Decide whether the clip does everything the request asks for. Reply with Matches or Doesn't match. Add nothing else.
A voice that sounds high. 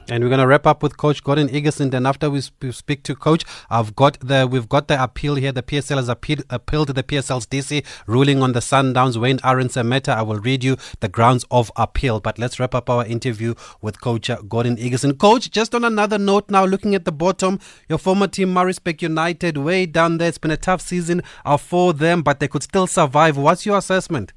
Doesn't match